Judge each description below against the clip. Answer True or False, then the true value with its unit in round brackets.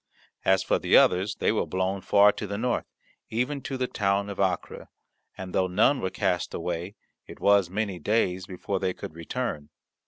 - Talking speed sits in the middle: True (185 wpm)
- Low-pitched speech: True (95 Hz)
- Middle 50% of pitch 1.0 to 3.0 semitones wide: True (2.4 semitones)